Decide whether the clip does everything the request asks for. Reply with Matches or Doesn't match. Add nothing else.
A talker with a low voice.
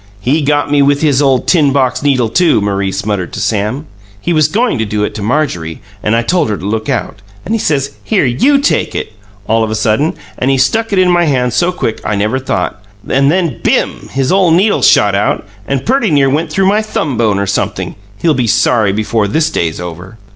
Matches